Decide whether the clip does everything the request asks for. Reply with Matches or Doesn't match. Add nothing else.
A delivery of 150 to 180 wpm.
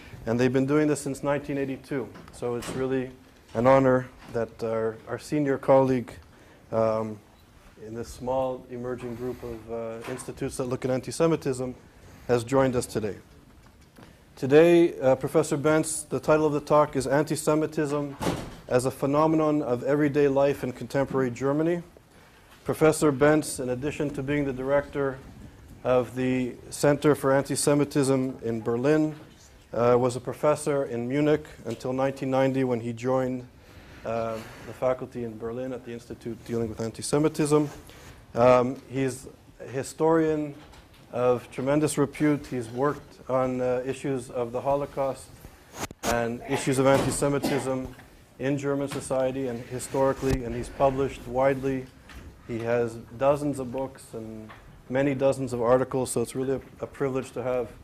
Doesn't match